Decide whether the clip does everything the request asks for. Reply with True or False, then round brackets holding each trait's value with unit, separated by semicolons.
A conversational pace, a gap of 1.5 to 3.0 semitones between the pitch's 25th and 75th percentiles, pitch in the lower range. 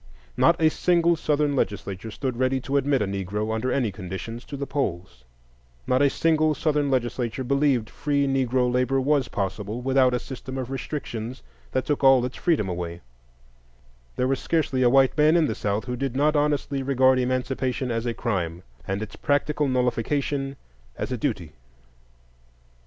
False (170 wpm; 3.6 semitones; 130 Hz)